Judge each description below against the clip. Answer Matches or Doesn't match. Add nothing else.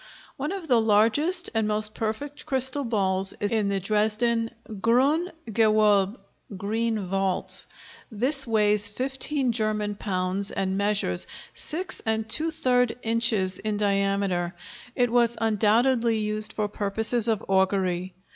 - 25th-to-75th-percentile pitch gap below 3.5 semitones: Matches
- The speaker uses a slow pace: Matches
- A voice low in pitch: Doesn't match